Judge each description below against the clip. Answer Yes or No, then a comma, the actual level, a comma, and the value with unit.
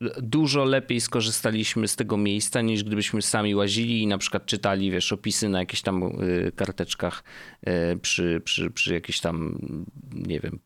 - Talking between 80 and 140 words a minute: No, average, 150 wpm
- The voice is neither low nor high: No, low, 105 Hz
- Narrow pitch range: No, average, 3.0 semitones